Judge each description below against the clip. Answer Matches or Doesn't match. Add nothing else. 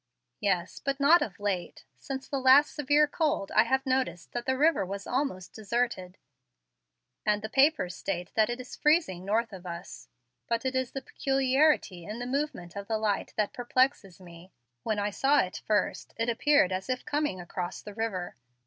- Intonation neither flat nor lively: Doesn't match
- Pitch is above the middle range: Matches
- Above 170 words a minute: Matches